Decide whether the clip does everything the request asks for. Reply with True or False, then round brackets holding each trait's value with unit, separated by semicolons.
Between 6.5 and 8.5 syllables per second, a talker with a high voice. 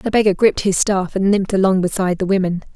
True (6.9 syllables/s; 195 Hz)